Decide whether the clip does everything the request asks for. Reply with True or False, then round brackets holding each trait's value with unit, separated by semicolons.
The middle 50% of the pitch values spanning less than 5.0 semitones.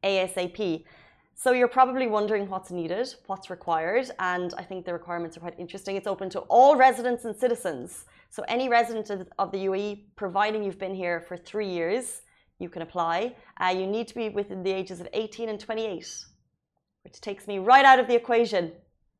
True (4.0 semitones)